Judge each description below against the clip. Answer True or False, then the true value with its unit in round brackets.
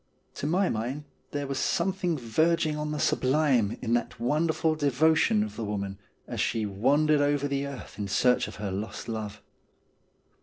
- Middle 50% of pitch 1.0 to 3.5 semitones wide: False (5.6 semitones)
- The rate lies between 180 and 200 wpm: False (165 wpm)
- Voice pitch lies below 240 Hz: True (140 Hz)